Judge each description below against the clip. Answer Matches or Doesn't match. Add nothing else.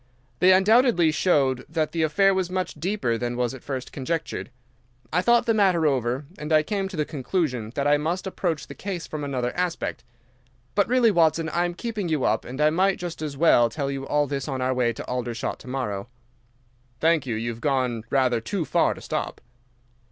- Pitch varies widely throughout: Matches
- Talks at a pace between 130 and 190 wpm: Doesn't match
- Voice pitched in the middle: Matches